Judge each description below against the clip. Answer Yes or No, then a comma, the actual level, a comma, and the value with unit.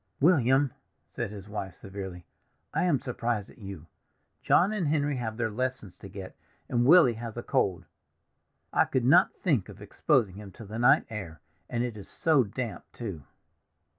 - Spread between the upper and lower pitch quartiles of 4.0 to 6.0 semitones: Yes, average, 4.9 semitones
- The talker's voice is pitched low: Yes, low, 115 Hz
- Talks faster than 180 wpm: No, average, 170 wpm